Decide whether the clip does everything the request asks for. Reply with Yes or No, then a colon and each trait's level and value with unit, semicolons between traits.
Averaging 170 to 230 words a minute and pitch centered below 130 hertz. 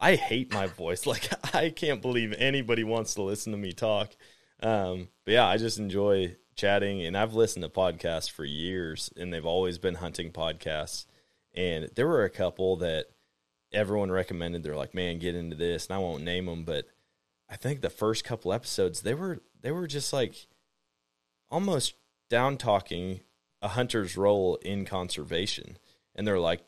Yes: average, 175 wpm; very low, 90 Hz